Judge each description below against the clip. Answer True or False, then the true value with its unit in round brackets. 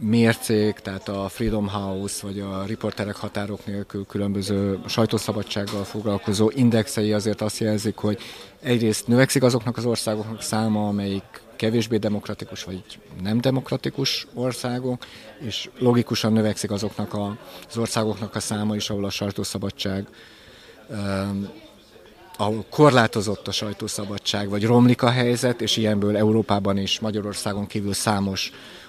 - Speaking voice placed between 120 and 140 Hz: False (105 Hz)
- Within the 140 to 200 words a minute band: False (120 wpm)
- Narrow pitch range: True (1.9 semitones)